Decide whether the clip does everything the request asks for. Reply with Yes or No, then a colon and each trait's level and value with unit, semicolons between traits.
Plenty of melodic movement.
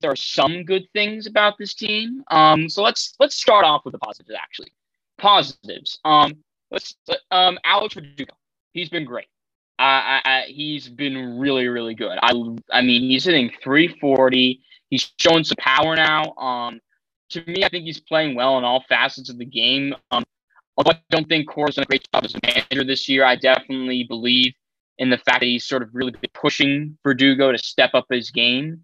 No: average, 4.4 semitones